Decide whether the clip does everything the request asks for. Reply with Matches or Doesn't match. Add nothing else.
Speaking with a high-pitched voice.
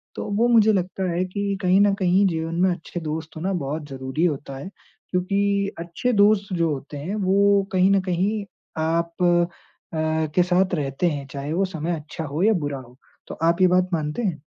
Doesn't match